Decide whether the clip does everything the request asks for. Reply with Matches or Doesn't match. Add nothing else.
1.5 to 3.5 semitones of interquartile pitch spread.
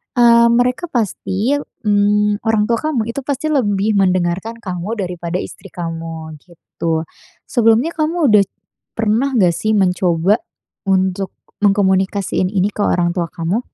Doesn't match